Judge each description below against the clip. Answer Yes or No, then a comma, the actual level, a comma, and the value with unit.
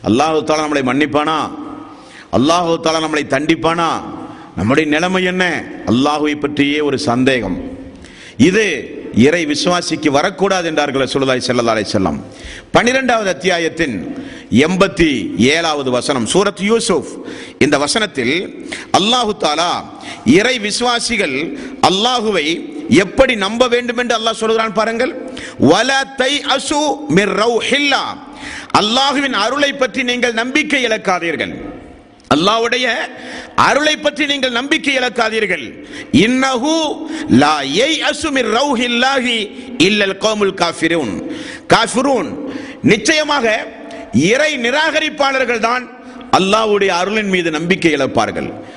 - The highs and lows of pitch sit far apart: Yes, wide, 7.5 semitones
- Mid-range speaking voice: No, high, 235 Hz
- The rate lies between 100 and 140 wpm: No, average, 85 wpm